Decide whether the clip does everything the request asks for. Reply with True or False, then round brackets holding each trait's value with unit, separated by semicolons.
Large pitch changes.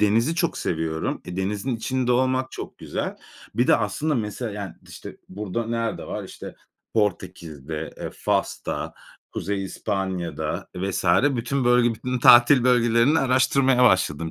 False (4.9 semitones)